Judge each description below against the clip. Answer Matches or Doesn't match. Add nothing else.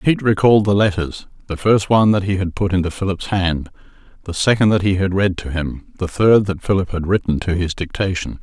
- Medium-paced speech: Doesn't match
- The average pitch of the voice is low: Matches